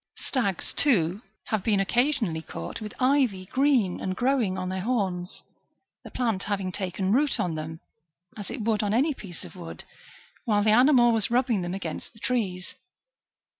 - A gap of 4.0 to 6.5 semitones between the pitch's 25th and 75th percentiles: Yes, average, 4.8 semitones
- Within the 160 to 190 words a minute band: Yes, average, 170 wpm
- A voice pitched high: Yes, high, 205 Hz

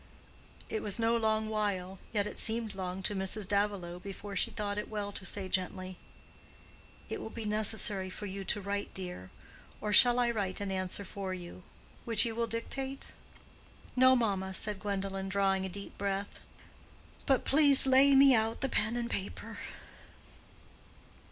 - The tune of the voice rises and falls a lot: No, average, 2.9 semitones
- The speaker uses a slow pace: No, average, 160 wpm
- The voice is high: Yes, high, 205 Hz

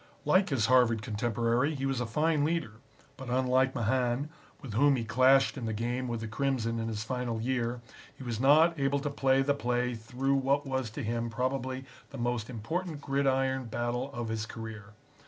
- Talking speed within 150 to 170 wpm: No, average, 190 wpm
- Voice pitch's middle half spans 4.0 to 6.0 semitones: No, average, 2.8 semitones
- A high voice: No, low, 125 Hz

